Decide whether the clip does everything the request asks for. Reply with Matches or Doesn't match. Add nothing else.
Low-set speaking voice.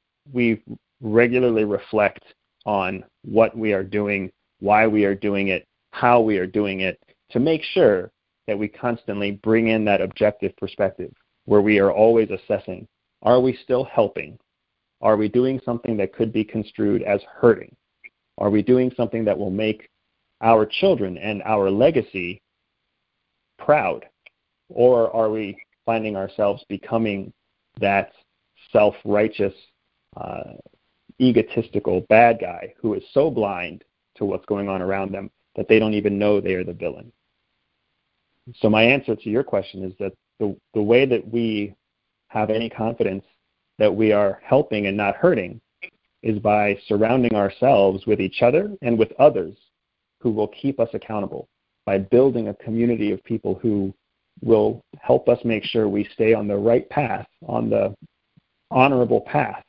Matches